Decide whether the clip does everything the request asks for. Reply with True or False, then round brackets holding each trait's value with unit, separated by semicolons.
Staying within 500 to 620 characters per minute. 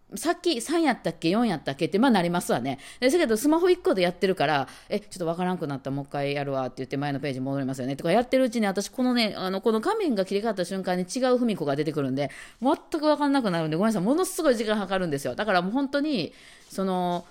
True (540 characters per minute)